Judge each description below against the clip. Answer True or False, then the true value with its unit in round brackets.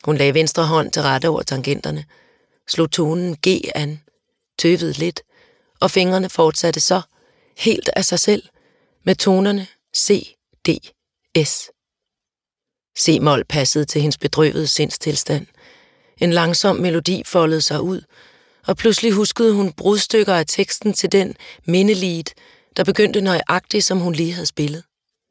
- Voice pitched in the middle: True (175 Hz)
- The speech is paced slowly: True (140 wpm)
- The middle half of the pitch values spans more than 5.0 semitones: False (3.9 semitones)